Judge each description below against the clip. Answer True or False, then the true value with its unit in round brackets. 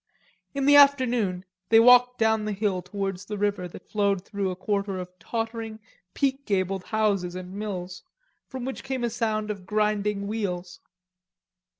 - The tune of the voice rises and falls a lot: False (2.9 semitones)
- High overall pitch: True (210 Hz)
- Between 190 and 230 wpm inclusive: False (160 wpm)